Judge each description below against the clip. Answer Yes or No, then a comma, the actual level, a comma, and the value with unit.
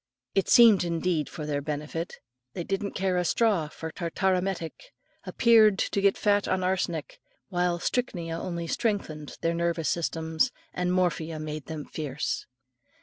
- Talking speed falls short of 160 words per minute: Yes, average, 145 wpm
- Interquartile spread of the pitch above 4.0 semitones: No, average, 3.2 semitones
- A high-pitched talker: No, medium, 175 Hz